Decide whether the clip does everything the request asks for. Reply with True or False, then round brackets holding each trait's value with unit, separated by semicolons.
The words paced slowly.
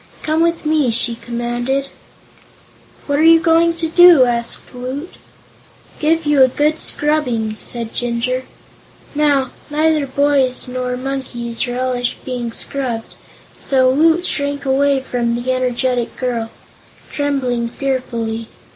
True (120 wpm)